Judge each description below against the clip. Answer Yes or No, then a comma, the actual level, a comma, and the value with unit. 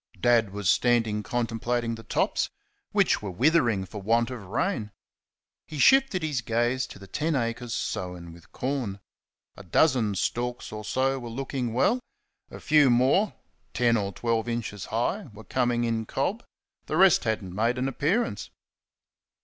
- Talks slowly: No, average, 155 wpm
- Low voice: Yes, low, 120 Hz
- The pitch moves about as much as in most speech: Yes, average, 3.8 semitones